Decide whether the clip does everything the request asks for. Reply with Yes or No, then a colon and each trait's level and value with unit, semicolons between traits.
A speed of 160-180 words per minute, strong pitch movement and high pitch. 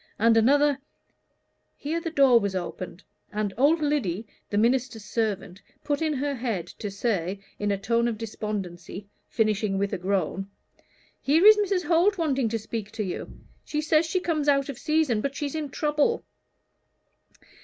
Yes: average, 165 wpm; wide, 6.4 semitones; high, 235 Hz